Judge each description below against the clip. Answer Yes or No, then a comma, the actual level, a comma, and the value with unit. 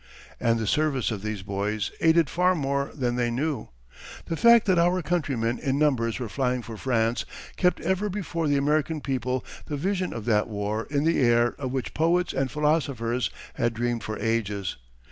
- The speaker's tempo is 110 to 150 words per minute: No, average, 185 wpm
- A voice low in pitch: Yes, low, 130 Hz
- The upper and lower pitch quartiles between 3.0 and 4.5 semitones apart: No, wide, 5.4 semitones